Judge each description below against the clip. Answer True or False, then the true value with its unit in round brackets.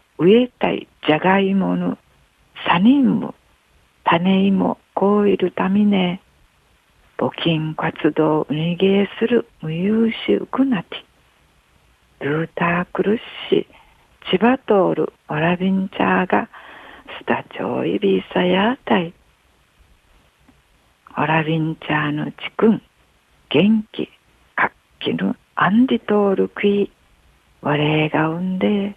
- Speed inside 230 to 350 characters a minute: False (215 characters per minute)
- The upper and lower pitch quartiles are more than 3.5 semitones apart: True (5.1 semitones)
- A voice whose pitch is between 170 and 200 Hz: True (185 Hz)